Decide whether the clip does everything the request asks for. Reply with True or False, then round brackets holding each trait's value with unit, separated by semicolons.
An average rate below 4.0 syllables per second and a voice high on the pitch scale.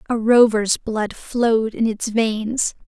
True (3.5 syllables/s; 225 Hz)